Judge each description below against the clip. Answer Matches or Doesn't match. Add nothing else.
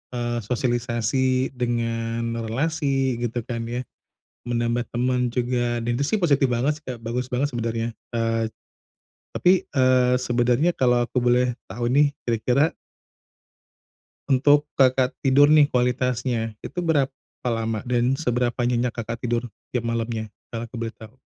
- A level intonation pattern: Matches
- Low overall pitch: Matches